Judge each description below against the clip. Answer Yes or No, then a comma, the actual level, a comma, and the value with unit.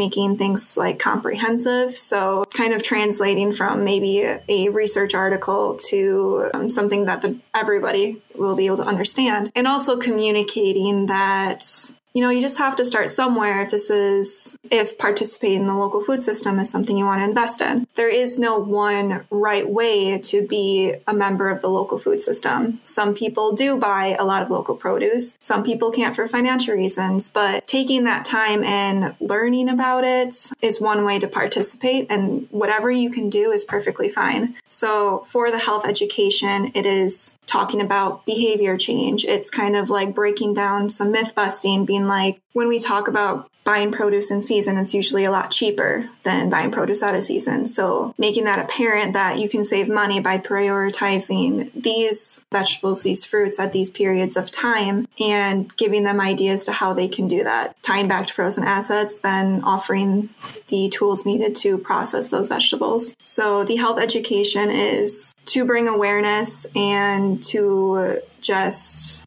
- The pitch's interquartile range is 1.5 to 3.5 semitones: Yes, average, 2.9 semitones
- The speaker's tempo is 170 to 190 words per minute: Yes, average, 175 wpm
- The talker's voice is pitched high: Yes, high, 210 Hz